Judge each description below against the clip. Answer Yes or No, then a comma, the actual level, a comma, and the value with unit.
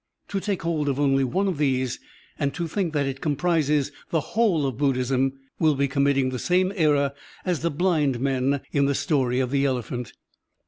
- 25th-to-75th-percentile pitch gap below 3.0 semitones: No, average, 3.5 semitones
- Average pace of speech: Yes, average, 190 wpm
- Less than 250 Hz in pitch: Yes, medium, 140 Hz